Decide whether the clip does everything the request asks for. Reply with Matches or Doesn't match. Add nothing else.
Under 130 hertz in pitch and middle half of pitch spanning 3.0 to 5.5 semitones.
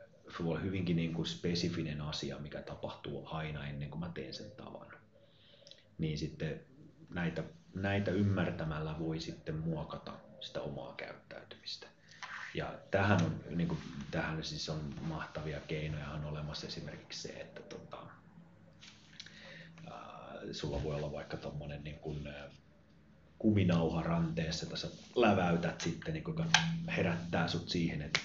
Matches